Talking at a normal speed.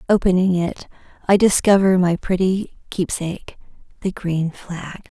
No: slow, 105 wpm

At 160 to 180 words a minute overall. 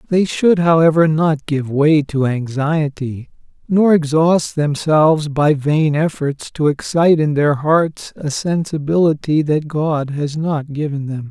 No: average, 145 wpm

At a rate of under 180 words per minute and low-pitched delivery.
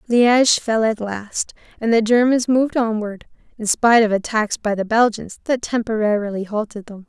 No: average, 170 wpm; high, 220 Hz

